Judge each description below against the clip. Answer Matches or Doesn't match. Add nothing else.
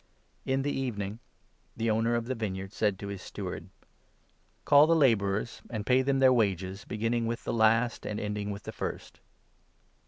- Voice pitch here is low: Matches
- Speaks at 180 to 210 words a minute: Matches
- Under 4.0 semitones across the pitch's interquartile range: Matches